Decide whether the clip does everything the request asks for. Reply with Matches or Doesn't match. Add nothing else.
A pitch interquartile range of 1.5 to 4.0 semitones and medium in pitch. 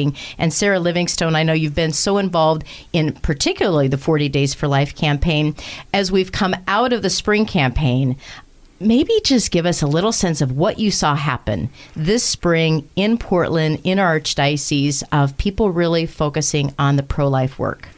Doesn't match